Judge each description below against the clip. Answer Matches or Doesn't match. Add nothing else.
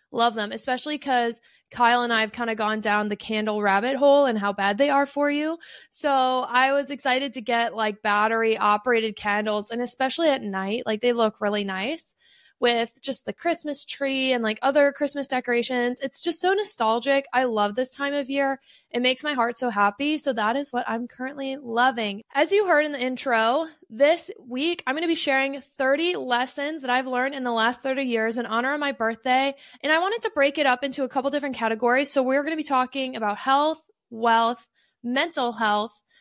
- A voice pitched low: Doesn't match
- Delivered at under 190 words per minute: Doesn't match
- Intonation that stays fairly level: Doesn't match